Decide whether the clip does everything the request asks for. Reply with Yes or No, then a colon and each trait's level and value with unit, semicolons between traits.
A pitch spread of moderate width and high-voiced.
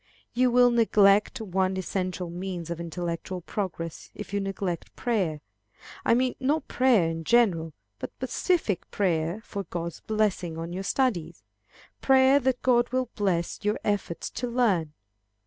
No: wide, 5.8 semitones; high, 195 Hz